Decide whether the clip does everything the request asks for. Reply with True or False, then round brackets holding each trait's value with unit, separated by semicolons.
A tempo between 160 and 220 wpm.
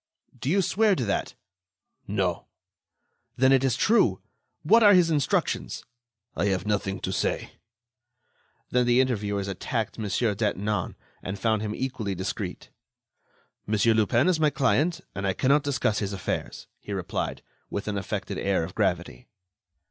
False (150 wpm)